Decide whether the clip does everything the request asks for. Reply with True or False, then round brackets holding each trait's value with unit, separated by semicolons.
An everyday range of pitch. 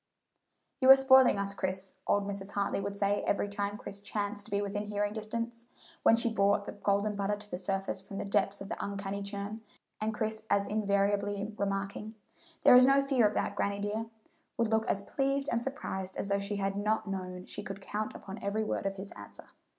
False (1.6 semitones)